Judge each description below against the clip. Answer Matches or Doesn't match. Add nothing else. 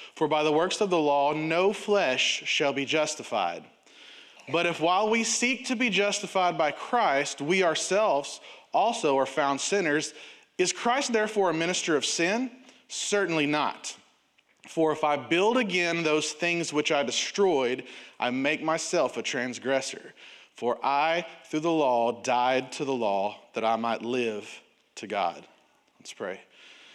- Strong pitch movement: Matches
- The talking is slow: Doesn't match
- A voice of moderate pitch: Matches